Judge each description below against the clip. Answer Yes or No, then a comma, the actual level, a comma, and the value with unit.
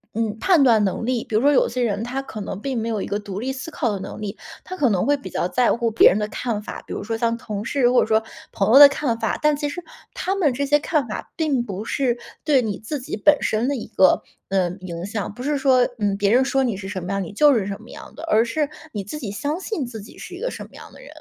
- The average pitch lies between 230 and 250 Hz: Yes, high, 235 Hz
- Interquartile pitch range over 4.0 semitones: Yes, average, 5.2 semitones